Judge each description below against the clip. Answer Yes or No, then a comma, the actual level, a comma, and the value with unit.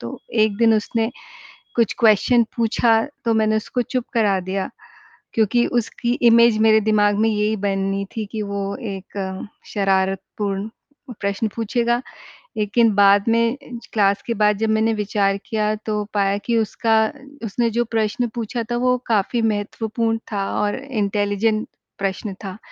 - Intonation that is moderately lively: No, narrow, 2.3 semitones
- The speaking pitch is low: No, high, 215 Hz